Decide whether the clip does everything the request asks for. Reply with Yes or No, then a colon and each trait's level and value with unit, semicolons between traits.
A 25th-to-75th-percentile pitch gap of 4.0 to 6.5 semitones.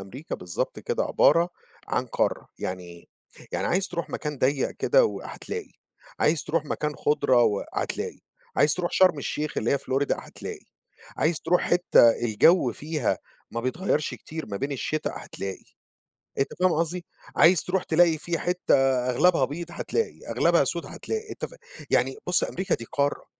Yes: average, 4.8 semitones